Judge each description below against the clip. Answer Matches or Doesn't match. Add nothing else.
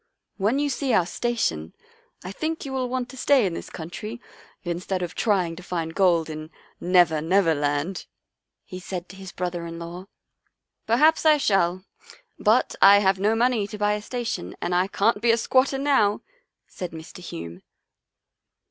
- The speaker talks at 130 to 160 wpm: Doesn't match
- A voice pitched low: Doesn't match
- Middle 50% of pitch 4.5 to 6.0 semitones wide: Matches